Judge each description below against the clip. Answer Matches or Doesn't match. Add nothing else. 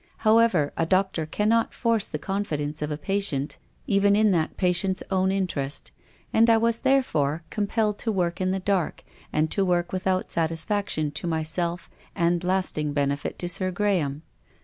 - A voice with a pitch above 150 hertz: Matches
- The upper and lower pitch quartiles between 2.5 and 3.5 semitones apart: Doesn't match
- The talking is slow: Doesn't match